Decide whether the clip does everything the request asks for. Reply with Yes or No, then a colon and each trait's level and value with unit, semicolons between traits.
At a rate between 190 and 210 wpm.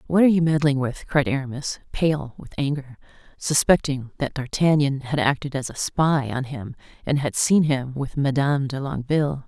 No: average, 175 wpm